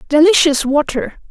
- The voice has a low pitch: No, very high, 305 Hz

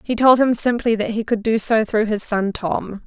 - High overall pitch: Yes, high, 225 Hz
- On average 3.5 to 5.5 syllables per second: Yes, 4.7 syllables/s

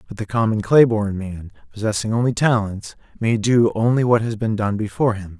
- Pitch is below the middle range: Yes, low, 110 Hz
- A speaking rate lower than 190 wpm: No, average, 200 wpm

